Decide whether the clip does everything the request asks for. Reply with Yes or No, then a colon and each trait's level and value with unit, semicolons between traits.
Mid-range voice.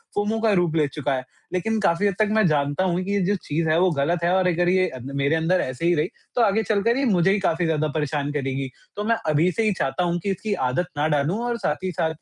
Yes: medium, 175 Hz